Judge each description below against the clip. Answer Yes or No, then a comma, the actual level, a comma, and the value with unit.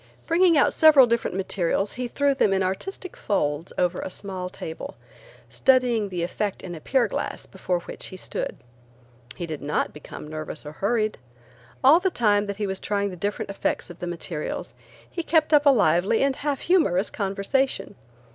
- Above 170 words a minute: Yes, average, 180 wpm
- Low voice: No, high, 200 Hz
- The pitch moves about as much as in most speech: No, wide, 6.8 semitones